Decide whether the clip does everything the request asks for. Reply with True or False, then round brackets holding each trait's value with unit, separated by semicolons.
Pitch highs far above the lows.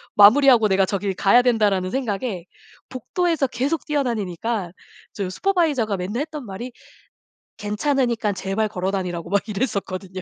False (4.9 semitones)